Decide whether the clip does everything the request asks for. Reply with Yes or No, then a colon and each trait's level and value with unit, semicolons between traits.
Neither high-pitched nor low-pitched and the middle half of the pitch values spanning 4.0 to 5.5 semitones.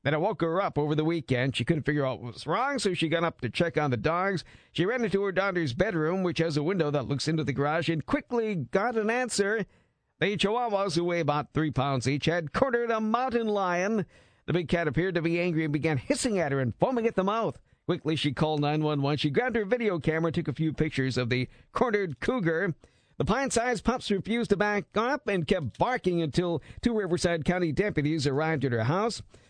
Yes: medium, 170 Hz; average, 5.2 semitones